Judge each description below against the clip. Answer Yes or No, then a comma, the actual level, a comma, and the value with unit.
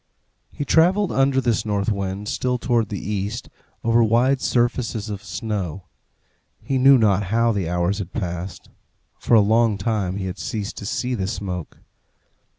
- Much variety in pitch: No, average, 3.4 semitones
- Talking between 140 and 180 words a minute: Yes, average, 160 wpm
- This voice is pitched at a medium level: No, low, 105 Hz